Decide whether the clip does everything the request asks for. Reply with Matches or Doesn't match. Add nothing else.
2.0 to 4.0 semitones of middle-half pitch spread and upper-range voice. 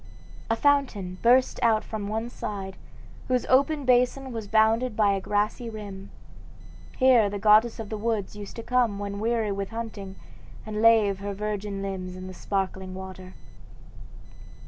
Matches